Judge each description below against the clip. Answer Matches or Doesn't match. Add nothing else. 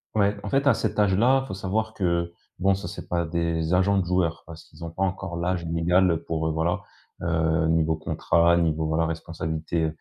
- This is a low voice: Matches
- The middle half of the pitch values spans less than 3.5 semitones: Matches